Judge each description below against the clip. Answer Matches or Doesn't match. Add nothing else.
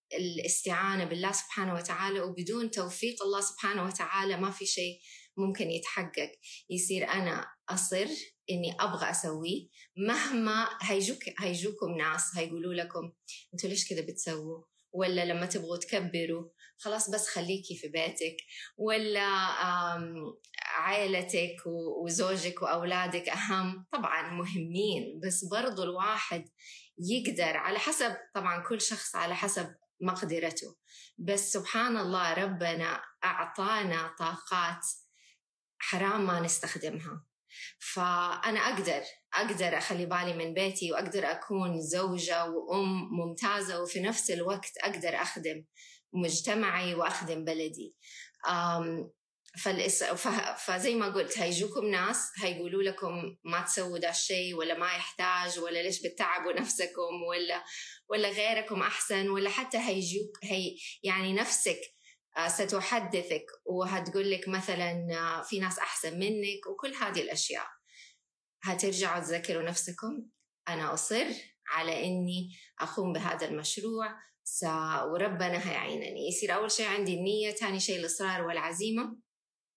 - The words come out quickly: Doesn't match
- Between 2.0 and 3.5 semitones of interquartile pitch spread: Matches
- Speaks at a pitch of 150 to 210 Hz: Matches